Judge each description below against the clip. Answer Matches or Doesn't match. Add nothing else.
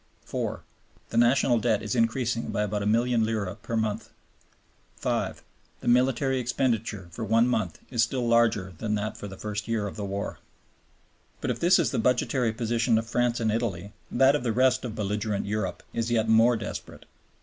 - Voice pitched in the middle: Doesn't match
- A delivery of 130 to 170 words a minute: Doesn't match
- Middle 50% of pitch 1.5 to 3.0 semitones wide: Matches